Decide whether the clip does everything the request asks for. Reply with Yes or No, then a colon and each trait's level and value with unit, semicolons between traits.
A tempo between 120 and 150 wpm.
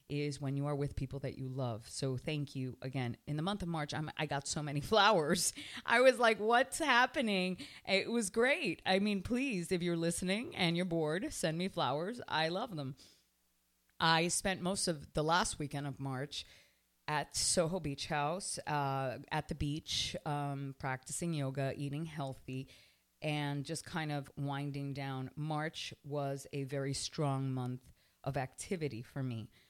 No: average, 170 wpm